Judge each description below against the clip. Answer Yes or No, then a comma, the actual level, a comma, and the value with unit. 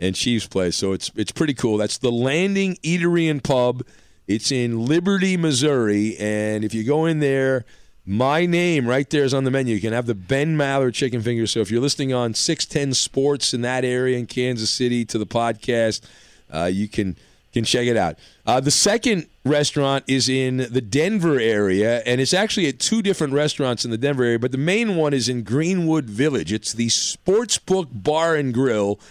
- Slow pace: No, average, 200 wpm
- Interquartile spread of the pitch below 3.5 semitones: No, average, 4.6 semitones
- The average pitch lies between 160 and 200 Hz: No, low, 130 Hz